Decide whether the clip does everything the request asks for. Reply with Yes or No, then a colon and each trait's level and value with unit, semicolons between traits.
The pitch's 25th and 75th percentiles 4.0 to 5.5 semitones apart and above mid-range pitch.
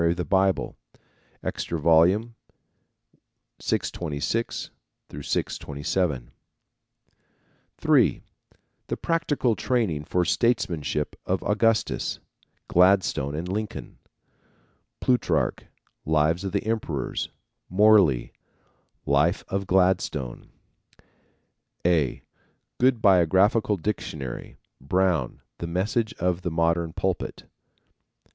No: average, 4.7 semitones; very low, 90 Hz